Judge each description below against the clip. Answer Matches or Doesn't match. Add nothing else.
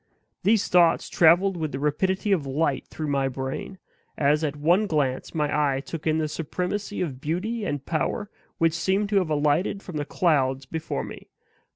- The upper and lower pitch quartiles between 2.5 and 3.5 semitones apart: Doesn't match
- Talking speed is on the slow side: Doesn't match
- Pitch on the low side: Doesn't match